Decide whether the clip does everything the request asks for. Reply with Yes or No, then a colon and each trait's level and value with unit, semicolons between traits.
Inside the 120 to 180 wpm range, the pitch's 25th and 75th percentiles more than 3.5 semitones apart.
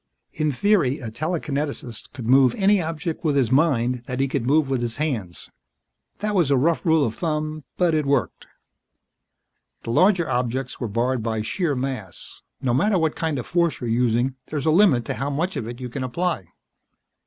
No: average, 190 wpm; average, 4.8 semitones